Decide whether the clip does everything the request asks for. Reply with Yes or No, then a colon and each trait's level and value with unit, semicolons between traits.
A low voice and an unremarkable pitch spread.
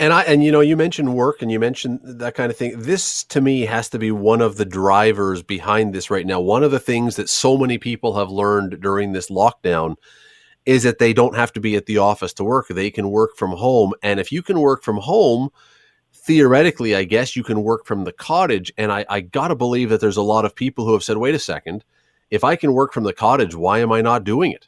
Yes: low, 115 Hz; average, 4.0 semitones